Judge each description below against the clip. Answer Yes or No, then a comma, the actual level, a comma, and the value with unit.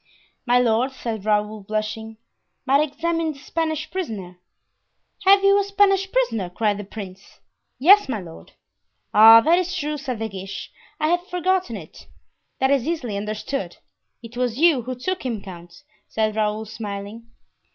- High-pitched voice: Yes, high, 235 Hz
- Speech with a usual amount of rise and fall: No, wide, 7.3 semitones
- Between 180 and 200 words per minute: No, average, 155 wpm